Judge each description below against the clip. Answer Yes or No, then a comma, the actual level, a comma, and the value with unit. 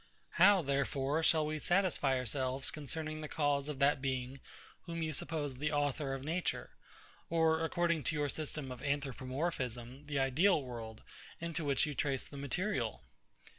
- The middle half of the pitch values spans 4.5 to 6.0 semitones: No, average, 3.0 semitones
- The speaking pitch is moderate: Yes, medium, 145 Hz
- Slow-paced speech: No, average, 155 wpm